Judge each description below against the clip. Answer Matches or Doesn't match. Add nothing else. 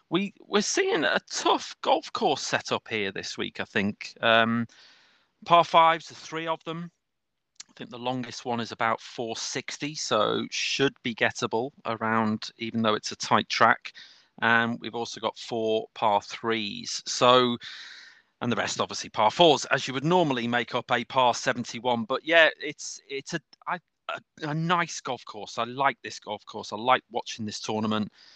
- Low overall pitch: Matches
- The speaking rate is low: Doesn't match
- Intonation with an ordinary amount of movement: Doesn't match